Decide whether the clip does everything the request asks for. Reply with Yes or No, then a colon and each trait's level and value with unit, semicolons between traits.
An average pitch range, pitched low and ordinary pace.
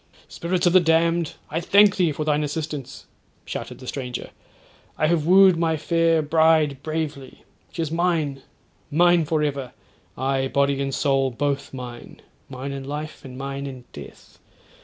No: average, 3.3 semitones; medium, 150 Hz; average, 150 wpm